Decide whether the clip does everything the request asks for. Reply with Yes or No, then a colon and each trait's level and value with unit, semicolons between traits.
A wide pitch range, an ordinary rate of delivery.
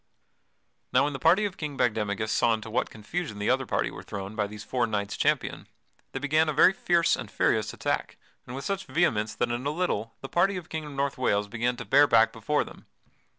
No: wide, 6.0 semitones; fast, 230 wpm